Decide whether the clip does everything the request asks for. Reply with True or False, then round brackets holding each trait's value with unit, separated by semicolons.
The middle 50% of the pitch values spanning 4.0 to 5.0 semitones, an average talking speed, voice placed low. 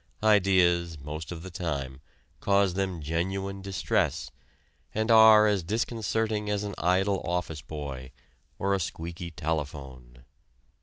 False (4.3 semitones; 120 wpm; 90 Hz)